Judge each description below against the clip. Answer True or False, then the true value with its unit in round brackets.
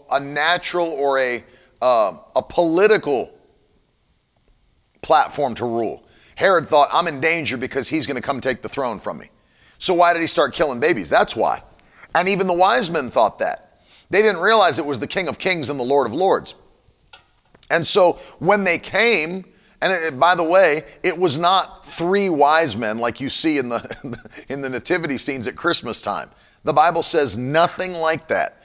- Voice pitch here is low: False (160 Hz)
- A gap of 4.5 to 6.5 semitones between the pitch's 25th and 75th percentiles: True (4.9 semitones)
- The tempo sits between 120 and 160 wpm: False (190 wpm)